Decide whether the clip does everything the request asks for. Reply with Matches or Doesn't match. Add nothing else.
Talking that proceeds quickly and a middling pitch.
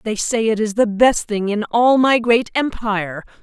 Doesn't match